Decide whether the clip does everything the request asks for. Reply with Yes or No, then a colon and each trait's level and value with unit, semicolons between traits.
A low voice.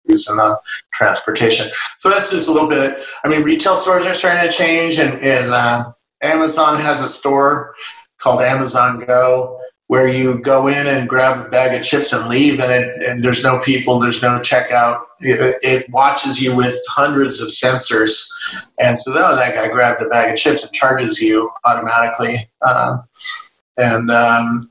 Yes: low, 130 Hz